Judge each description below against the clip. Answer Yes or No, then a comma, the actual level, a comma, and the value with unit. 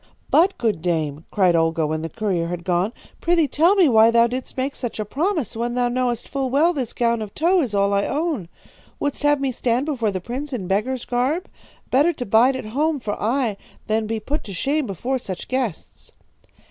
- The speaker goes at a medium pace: No, fast, 210 wpm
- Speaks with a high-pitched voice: Yes, high, 240 Hz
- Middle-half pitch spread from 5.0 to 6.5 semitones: Yes, wide, 5.6 semitones